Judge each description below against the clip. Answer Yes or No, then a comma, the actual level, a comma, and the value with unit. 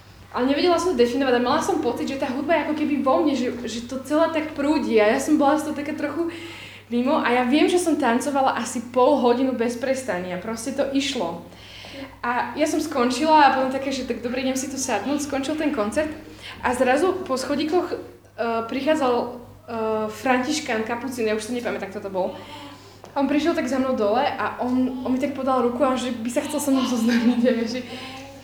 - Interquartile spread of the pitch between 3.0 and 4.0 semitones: Yes, average, 3.4 semitones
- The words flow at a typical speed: No, fast, 215 wpm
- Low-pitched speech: No, very high, 260 Hz